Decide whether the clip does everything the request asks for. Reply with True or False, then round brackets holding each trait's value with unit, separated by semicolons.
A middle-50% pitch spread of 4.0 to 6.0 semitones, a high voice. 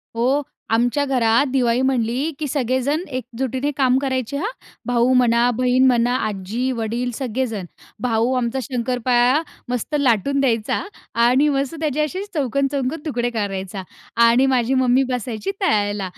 False (2.5 semitones; 250 Hz)